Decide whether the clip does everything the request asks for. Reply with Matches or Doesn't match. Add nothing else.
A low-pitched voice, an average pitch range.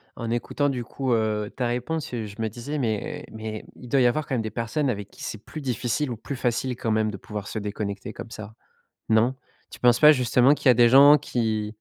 Matches